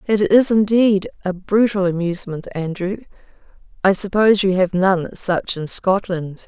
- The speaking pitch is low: No, high, 190 Hz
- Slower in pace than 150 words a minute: Yes, average, 140 wpm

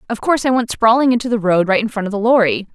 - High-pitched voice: Yes, high, 220 Hz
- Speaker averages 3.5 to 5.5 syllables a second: No, 7.1 syllables/s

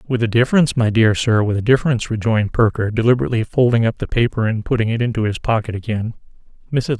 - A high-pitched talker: No, low, 115 Hz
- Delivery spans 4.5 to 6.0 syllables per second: No, 6.3 syllables/s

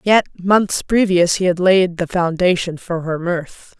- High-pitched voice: No, medium, 180 Hz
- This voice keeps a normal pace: Yes, average, 175 wpm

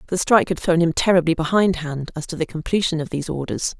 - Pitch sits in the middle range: Yes, medium, 170 Hz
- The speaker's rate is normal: No, fast, 220 wpm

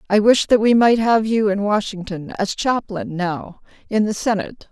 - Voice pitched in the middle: No, high, 210 Hz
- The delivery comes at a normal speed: Yes, average, 180 wpm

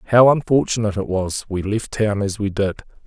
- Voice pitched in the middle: No, low, 105 Hz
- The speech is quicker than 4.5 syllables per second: Yes, 5.6 syllables/s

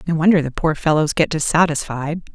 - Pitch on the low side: No, medium, 155 Hz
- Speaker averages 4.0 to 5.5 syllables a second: No, 5.7 syllables/s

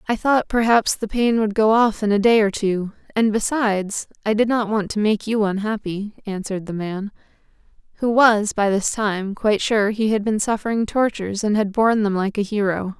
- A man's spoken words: No, female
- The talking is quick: Yes, fast, 210 wpm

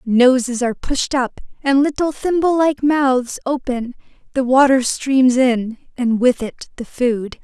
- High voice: Yes, very high, 260 Hz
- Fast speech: No, average, 155 wpm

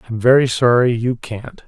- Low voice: Yes, low, 120 Hz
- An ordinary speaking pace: No, fast, 215 wpm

